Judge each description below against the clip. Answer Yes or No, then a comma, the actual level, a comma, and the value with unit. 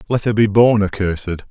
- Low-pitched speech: Yes, low, 100 Hz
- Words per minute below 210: Yes, average, 200 wpm